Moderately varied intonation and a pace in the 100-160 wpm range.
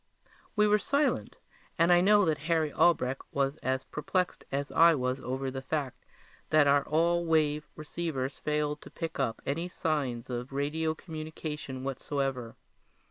Yes: average, 3.4 semitones; average, 150 wpm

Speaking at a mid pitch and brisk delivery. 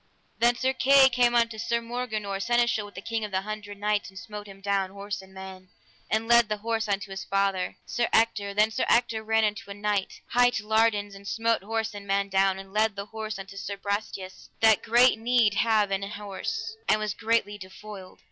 No: high, 210 Hz; fast, 210 wpm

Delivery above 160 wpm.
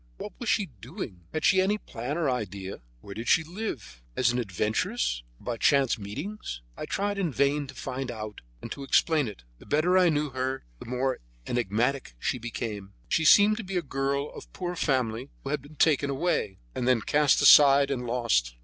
Yes: average, 200 wpm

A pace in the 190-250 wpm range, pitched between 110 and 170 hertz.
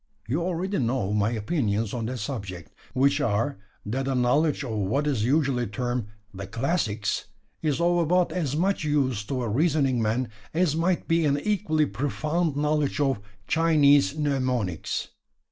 No: average, 155 wpm; medium, 140 Hz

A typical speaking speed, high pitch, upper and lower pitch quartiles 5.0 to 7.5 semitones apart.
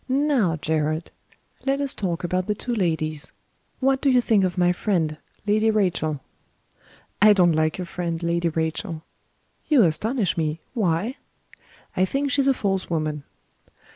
No: average, 150 wpm; medium, 180 Hz; wide, 5.6 semitones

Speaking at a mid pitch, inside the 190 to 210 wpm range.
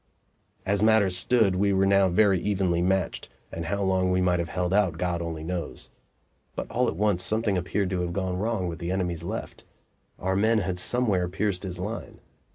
No: very low, 95 Hz; average, 195 wpm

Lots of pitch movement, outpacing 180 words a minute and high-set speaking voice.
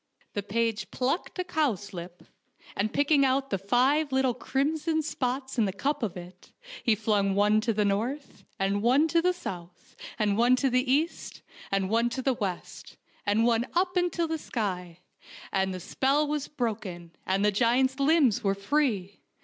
No: wide, 5.8 semitones; average, 175 wpm; high, 235 Hz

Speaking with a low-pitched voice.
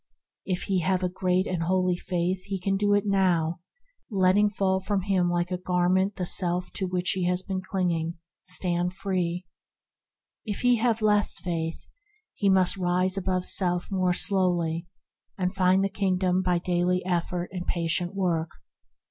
No: medium, 185 Hz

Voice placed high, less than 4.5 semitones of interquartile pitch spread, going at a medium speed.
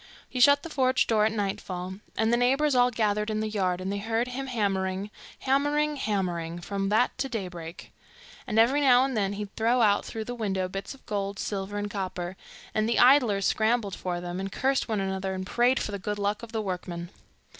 No: high, 210 Hz; average, 4.1 semitones; fast, 210 wpm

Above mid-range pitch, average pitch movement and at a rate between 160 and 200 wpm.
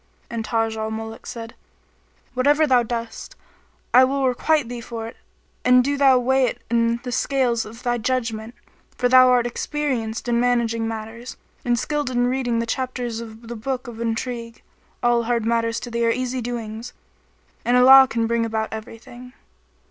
No: high, 240 Hz; narrow, 1.8 semitones; average, 170 wpm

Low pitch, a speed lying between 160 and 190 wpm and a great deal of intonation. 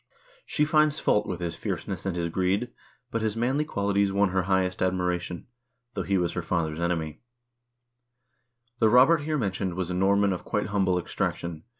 No: very low, 95 Hz; average, 180 wpm; average, 2.8 semitones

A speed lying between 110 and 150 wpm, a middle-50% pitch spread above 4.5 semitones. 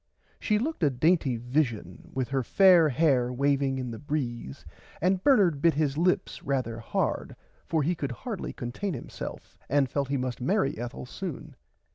No: average, 175 wpm; average, 5.2 semitones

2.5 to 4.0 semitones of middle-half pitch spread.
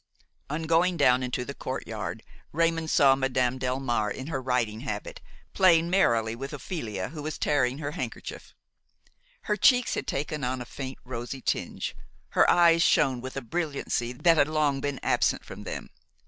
No: average, 4.5 semitones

